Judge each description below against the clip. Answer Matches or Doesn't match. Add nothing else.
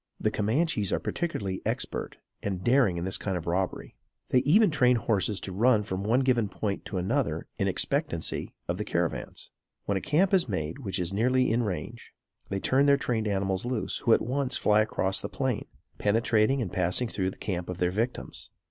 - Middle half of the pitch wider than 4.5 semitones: Matches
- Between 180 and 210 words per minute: Matches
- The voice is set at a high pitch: Doesn't match